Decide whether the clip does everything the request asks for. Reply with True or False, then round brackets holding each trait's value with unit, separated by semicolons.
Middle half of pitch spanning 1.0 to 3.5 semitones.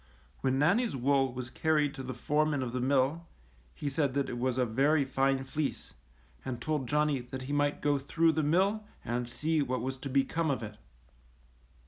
True (2.7 semitones)